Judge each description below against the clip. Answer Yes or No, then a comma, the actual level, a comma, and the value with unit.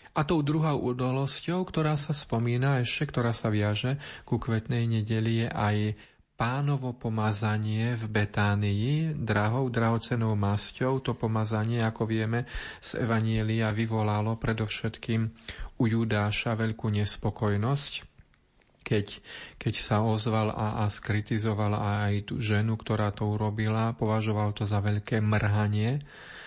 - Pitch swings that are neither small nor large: No, narrow, 2.3 semitones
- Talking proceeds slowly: No, average, 120 wpm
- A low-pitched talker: Yes, low, 110 Hz